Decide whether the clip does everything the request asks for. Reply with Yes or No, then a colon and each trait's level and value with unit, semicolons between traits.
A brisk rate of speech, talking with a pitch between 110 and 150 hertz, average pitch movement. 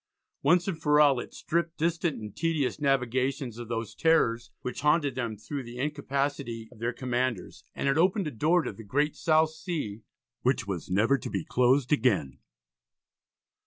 No: average, 170 wpm; low, 135 Hz; average, 4.6 semitones